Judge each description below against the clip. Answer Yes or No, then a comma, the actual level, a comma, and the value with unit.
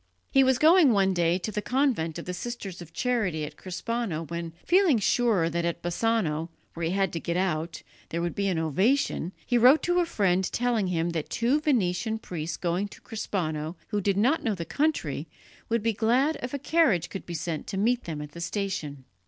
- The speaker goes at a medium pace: No, fast, 210 wpm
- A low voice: No, high, 195 Hz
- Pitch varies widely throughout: Yes, wide, 6.1 semitones